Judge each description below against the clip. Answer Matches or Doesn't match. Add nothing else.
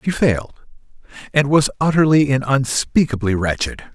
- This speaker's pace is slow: Matches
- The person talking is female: Doesn't match